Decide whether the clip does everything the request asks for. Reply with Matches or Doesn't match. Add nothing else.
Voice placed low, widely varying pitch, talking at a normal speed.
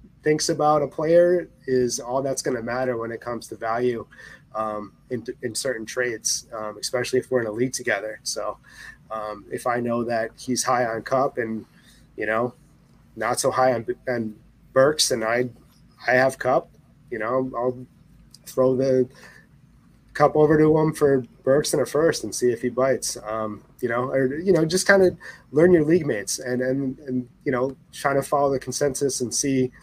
Doesn't match